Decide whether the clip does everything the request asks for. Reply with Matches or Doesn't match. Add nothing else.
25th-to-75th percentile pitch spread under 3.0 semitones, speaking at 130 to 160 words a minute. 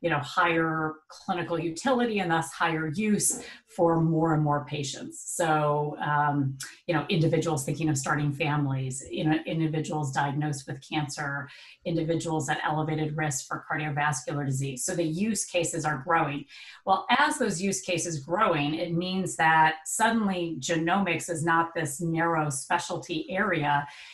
Matches